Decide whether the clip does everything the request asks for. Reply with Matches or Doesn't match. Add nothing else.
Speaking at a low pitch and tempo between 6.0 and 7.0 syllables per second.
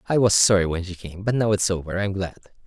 Matches